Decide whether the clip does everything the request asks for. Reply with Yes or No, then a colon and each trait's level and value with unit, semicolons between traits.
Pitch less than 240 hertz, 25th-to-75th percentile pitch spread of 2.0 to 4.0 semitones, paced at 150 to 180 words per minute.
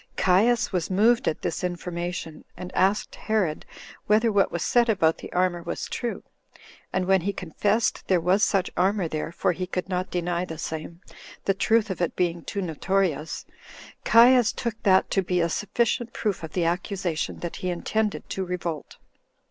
Yes: medium, 185 Hz; average, 3.2 semitones; average, 175 wpm